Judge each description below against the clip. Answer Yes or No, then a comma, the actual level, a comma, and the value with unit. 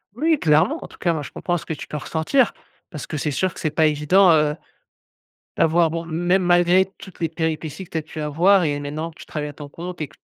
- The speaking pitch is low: No, medium, 160 Hz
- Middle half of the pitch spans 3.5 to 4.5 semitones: No, average, 2.8 semitones